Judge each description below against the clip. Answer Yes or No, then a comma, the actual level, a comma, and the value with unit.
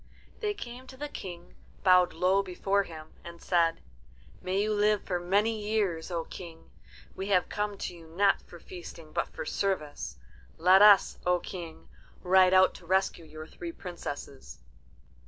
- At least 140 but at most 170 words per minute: Yes, average, 160 wpm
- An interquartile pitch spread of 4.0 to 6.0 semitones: No, average, 3.0 semitones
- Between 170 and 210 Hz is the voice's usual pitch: Yes, medium, 185 Hz